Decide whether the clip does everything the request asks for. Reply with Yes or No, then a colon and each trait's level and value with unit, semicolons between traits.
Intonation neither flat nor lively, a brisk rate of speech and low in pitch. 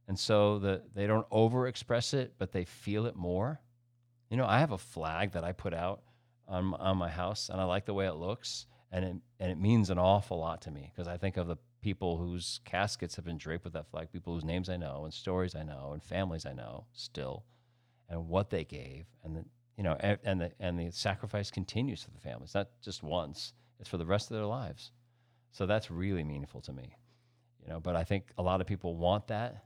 Yes: average, 4.9 semitones; fast, 235 wpm; very low, 95 Hz